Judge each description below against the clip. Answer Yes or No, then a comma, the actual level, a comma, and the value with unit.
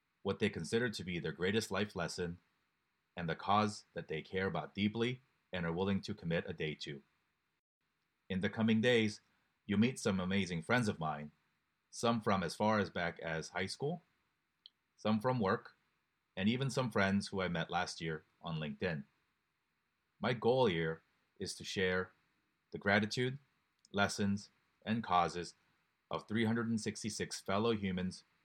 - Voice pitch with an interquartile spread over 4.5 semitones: No, average, 3.6 semitones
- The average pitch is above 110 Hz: No, low, 100 Hz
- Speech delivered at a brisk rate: No, average, 155 wpm